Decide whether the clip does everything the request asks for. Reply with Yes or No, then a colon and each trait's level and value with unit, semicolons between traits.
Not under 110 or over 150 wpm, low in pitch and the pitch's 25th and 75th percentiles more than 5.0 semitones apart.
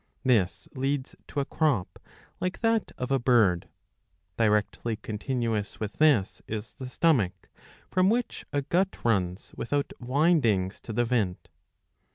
Yes: slow, 135 wpm; low, 120 Hz; wide, 5.4 semitones